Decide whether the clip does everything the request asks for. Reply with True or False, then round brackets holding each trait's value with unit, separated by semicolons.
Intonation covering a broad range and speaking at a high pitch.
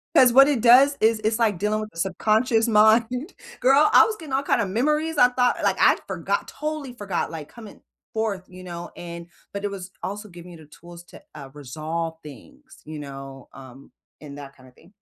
True (6.9 semitones; 210 Hz)